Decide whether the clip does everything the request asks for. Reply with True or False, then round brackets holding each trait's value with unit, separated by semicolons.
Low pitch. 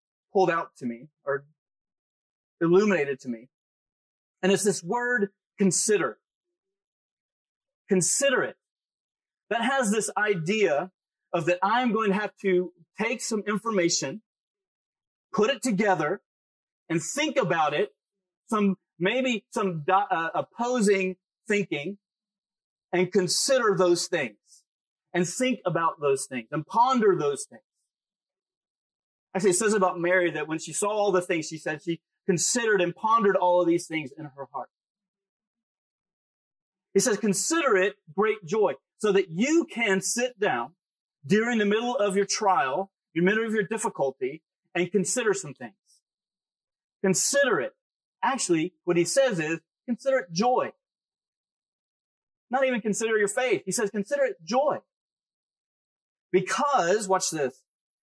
False (195 Hz)